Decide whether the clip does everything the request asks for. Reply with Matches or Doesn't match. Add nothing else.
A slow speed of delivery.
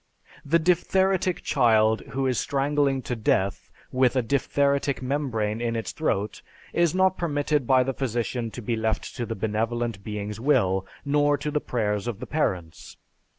Doesn't match